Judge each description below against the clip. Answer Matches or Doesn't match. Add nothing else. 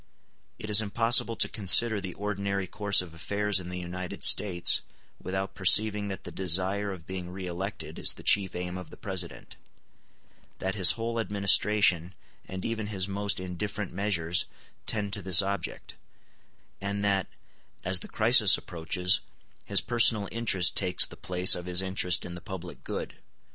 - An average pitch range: Doesn't match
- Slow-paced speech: Doesn't match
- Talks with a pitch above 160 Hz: Doesn't match